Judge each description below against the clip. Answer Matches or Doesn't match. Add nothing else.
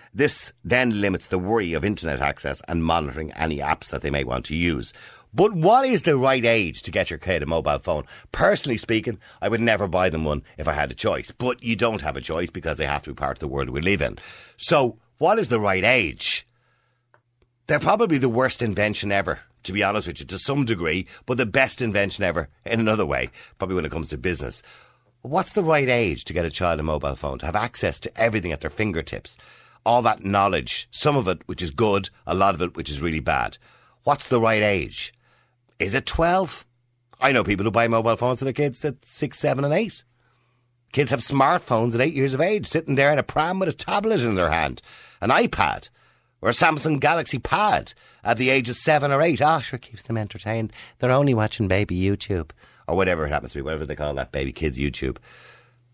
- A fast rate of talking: Matches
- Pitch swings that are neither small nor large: Doesn't match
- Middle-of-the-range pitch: Doesn't match